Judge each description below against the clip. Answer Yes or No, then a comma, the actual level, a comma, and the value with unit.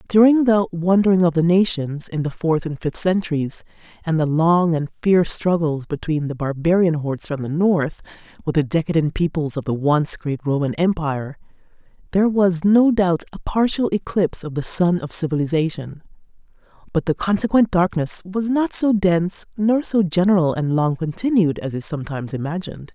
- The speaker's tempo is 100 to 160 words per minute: No, average, 170 wpm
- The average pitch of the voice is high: No, medium, 170 Hz